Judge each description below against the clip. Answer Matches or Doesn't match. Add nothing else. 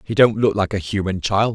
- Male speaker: Matches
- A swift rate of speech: Matches